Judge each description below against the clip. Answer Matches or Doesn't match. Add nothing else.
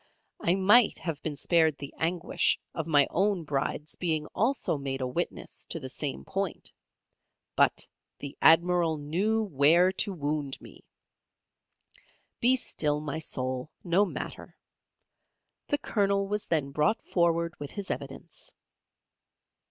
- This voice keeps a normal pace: Doesn't match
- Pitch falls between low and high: Matches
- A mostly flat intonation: Doesn't match